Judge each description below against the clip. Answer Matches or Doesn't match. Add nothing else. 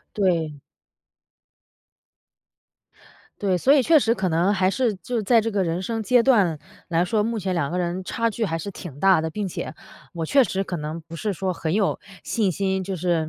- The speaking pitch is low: Doesn't match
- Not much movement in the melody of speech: Doesn't match